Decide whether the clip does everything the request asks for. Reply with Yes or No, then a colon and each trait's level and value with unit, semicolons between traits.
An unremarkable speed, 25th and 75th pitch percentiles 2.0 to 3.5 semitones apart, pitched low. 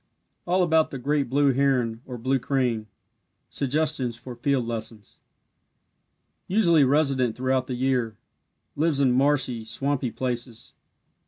No: slow, 120 wpm; average, 2.9 semitones; low, 130 Hz